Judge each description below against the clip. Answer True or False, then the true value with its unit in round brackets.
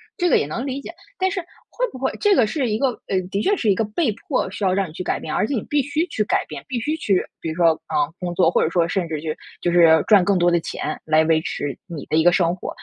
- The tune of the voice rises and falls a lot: True (7.6 semitones)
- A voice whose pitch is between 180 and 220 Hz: True (190 Hz)